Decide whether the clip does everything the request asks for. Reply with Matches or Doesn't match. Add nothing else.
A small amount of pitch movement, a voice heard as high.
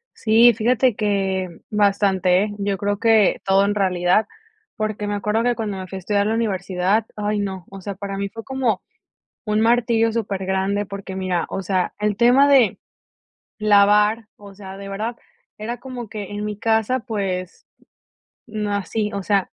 Matches